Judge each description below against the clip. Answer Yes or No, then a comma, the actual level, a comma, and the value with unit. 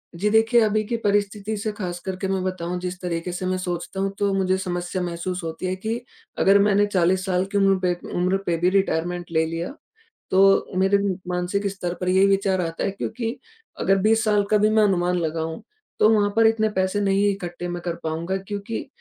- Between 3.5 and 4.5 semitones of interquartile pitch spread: No, narrow, 2.5 semitones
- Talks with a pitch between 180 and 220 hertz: Yes, high, 190 Hz